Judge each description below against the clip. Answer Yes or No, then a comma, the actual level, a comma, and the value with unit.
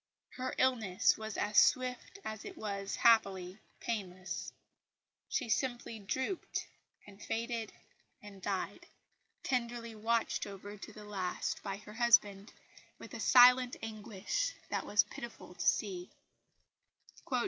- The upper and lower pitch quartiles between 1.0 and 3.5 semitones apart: Yes, average, 3.1 semitones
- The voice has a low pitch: No, high, 215 Hz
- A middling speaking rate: No, slow, 120 wpm